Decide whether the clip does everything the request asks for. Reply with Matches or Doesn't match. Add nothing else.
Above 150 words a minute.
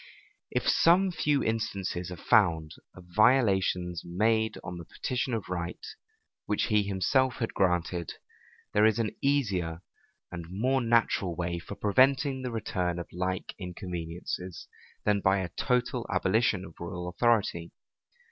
Doesn't match